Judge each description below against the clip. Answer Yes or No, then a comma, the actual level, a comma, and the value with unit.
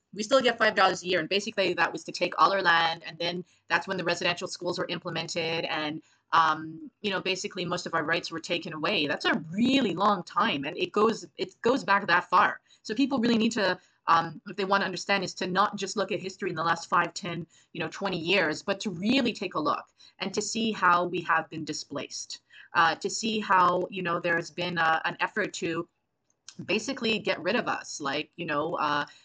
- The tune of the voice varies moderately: Yes, average, 3.1 semitones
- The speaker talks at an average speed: No, fast, 230 wpm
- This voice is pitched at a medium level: Yes, medium, 180 Hz